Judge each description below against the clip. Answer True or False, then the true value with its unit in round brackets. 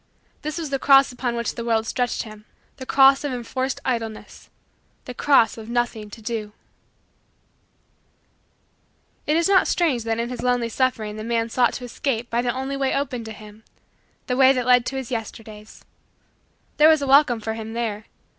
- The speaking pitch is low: False (240 Hz)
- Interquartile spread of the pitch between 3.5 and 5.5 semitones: False (3.1 semitones)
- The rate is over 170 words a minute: True (185 wpm)